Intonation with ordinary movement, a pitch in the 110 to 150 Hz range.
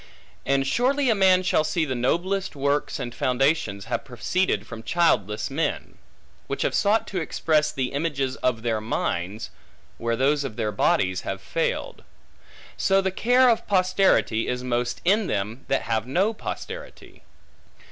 No: wide, 7.9 semitones; medium, 140 Hz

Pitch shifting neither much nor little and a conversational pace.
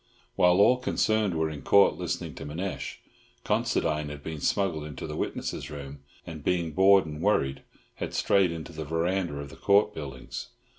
Yes: average, 4.7 semitones; average, 170 wpm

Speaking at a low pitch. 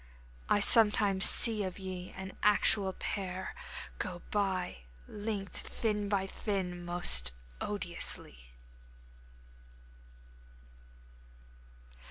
No: high, 195 Hz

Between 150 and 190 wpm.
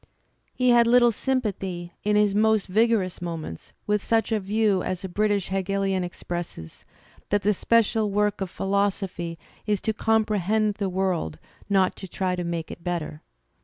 Yes: average, 160 wpm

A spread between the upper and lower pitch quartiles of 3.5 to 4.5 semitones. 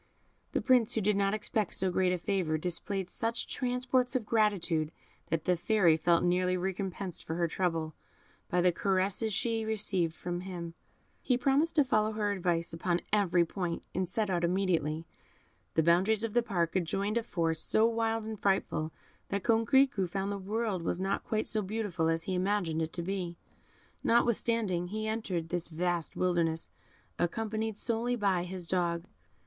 Yes: average, 4.0 semitones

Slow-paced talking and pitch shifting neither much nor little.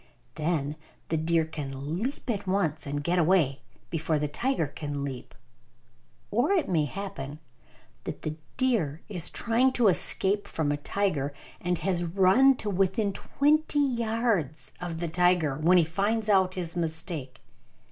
No: average, 150 wpm; average, 4.9 semitones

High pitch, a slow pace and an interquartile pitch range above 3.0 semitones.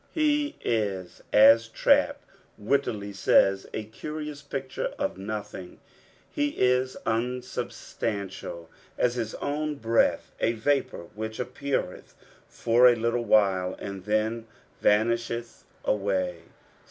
No: low, 115 Hz; slow, 110 wpm; average, 3.7 semitones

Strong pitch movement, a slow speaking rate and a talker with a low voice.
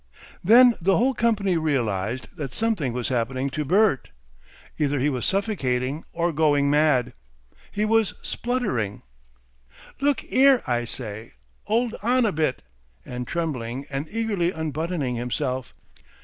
No: wide, 8.7 semitones; slow, 130 wpm; medium, 150 Hz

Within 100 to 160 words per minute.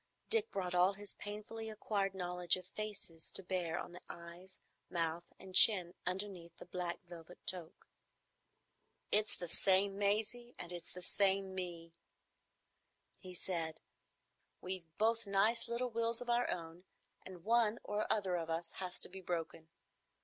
Yes: average, 150 wpm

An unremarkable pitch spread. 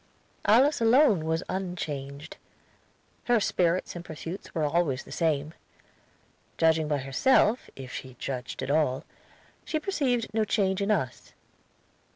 No: wide, 6.8 semitones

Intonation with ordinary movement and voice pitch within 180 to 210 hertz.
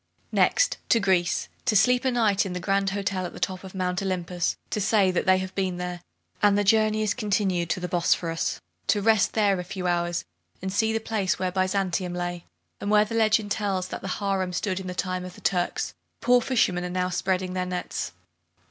No: narrow, 2.3 semitones; high, 190 Hz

